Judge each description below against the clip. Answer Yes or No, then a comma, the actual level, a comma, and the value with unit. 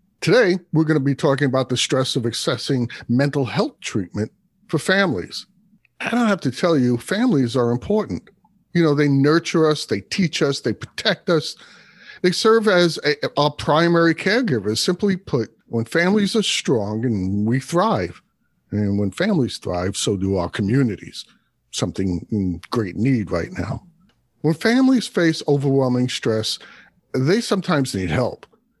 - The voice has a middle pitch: Yes, medium, 145 Hz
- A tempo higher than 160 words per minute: No, average, 155 wpm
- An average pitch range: No, wide, 7.8 semitones